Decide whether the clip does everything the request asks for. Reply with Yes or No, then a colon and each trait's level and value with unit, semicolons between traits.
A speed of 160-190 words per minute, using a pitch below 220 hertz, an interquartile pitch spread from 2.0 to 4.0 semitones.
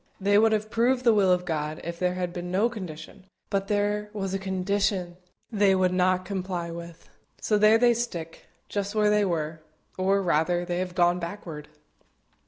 Yes: average, 185 wpm; medium, 185 Hz; average, 2.9 semitones